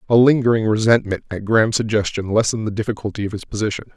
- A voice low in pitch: Yes, low, 110 Hz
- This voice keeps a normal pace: Yes, average, 180 wpm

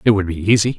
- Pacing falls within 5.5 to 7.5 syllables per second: Yes, 7.3 syllables/s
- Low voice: Yes, low, 100 Hz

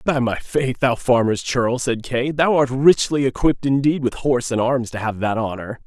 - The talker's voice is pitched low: Yes, low, 125 Hz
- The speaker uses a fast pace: Yes, fast, 215 wpm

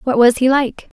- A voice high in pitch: Yes, very high, 260 Hz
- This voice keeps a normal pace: No, fast, 245 wpm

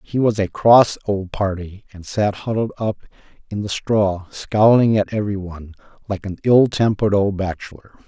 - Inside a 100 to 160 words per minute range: No, average, 170 wpm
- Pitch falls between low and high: No, low, 100 Hz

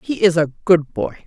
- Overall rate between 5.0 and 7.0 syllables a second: Yes, 5.1 syllables/s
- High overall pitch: No, medium, 170 Hz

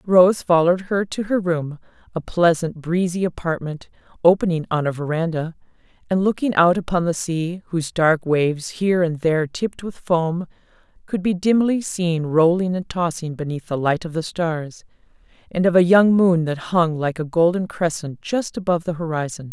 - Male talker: No, female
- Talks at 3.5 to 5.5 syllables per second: Yes, 5.0 syllables/s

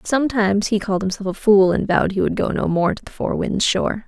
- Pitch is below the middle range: No, high, 205 Hz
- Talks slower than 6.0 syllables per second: No, 6.3 syllables/s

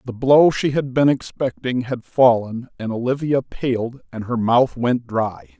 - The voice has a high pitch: No, low, 125 Hz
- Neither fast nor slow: Yes, average, 170 wpm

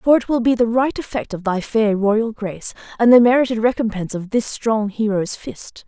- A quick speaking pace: Yes, fast, 215 wpm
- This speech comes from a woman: Yes, female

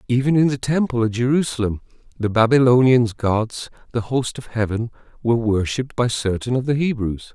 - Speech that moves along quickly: No, average, 165 wpm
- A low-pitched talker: Yes, low, 120 Hz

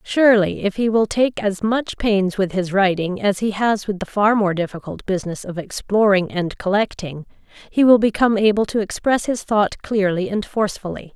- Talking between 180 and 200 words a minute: Yes, average, 190 wpm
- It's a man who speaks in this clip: No, female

